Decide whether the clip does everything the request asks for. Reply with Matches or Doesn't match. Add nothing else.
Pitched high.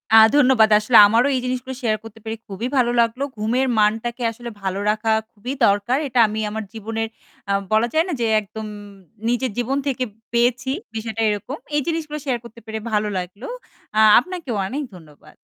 Matches